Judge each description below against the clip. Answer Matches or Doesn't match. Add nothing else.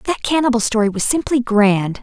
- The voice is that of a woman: Matches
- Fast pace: Doesn't match